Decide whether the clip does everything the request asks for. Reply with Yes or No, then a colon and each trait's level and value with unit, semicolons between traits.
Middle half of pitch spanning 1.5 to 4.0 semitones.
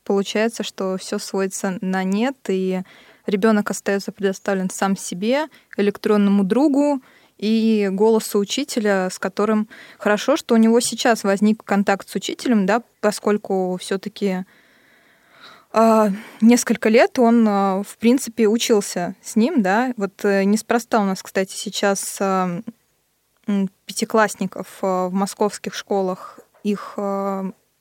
Yes: average, 2.7 semitones